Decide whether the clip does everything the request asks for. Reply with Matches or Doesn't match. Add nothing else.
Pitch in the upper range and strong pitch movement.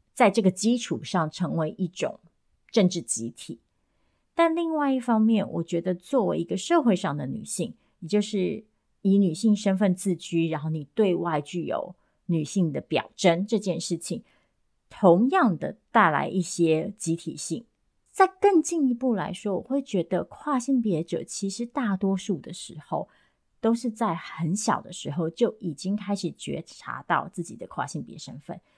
Doesn't match